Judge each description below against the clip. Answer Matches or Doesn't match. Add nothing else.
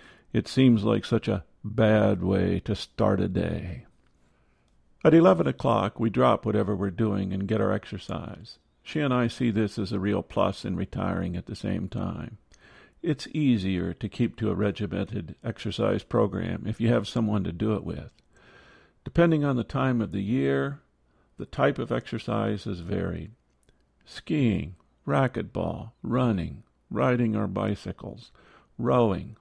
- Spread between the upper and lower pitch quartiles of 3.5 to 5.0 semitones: Doesn't match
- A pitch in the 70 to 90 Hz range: Doesn't match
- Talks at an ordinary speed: Matches